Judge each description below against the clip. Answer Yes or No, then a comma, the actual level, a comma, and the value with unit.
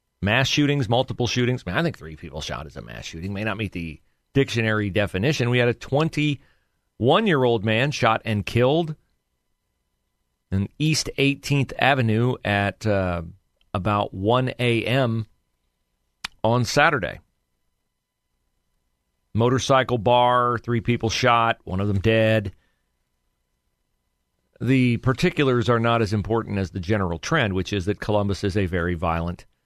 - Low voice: Yes, low, 110 Hz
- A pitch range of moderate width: No, wide, 6.1 semitones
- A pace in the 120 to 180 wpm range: Yes, slow, 135 wpm